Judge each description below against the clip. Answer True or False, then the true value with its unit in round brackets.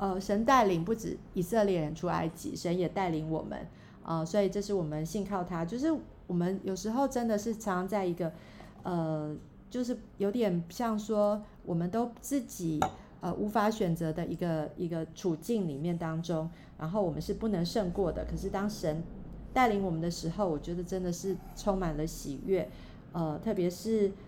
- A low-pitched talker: False (180 Hz)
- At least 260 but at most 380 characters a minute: True (265 characters per minute)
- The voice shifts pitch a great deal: False (4.0 semitones)